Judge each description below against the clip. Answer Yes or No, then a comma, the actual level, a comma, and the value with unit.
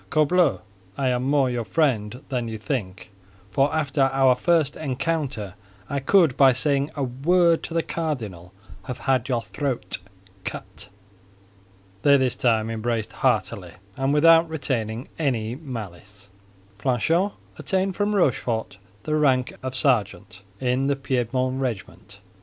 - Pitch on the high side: No, low, 130 Hz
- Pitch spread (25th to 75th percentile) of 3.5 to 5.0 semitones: Yes, average, 4.6 semitones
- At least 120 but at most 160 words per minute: Yes, slow, 135 wpm